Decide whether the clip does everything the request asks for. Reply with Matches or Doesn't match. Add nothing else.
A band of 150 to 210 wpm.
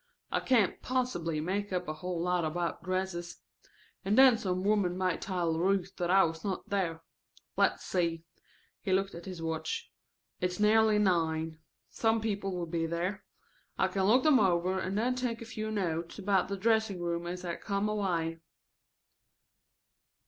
Matches